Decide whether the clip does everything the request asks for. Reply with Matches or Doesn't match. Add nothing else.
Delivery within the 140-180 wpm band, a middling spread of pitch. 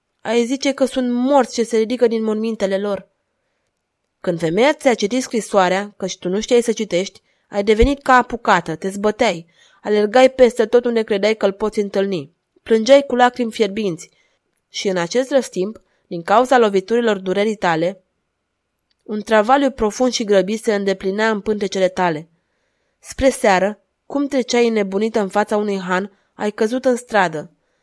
Matches